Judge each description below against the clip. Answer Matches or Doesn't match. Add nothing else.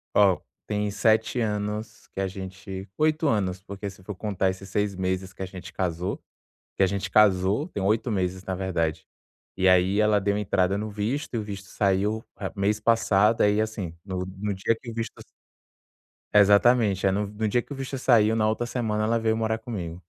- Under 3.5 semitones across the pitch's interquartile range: Matches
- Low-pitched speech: Matches